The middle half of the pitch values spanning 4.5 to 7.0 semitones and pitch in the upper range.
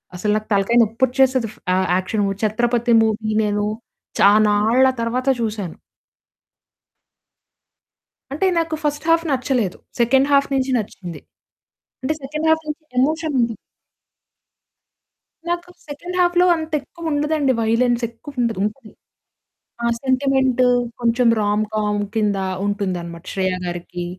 Yes: average, 5.2 semitones; high, 240 Hz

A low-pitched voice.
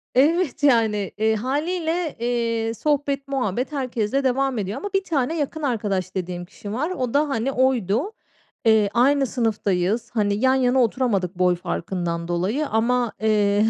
No: high, 240 Hz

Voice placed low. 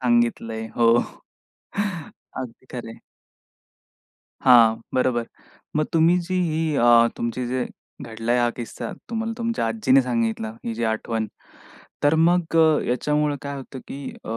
Yes: low, 125 Hz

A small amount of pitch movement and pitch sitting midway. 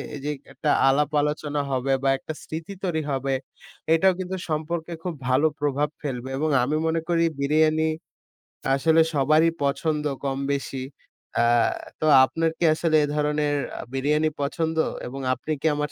Yes: narrow, 2.3 semitones; medium, 150 Hz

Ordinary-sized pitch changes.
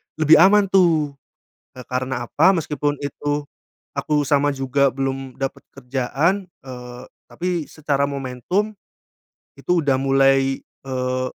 Yes: average, 3.0 semitones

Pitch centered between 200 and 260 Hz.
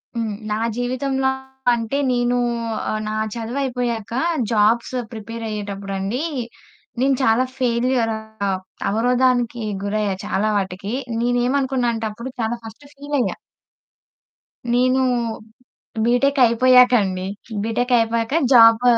Yes: high, 235 Hz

